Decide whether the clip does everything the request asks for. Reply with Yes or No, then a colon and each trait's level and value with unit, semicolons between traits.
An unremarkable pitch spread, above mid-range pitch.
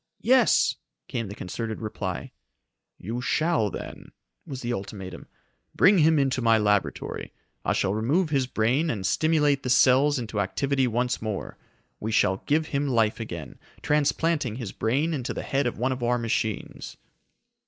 No: average, 4.9 semitones; low, 125 Hz